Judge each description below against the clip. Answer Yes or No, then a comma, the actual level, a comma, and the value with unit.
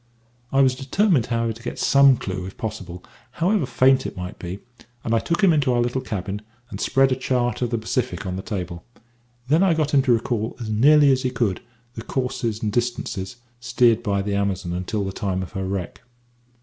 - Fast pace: Yes, fast, 210 wpm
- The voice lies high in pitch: No, low, 115 Hz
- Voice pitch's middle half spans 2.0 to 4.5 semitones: No, average, 4.9 semitones